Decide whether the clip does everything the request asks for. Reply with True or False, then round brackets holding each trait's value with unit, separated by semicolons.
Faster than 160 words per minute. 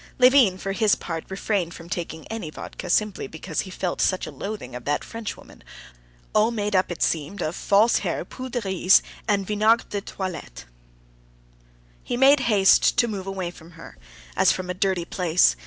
True (180 wpm)